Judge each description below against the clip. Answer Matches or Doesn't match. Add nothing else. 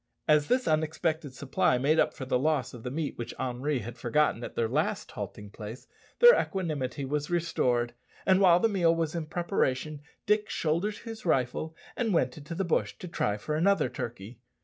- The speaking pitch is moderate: Matches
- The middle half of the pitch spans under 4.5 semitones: Doesn't match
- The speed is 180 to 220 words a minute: Matches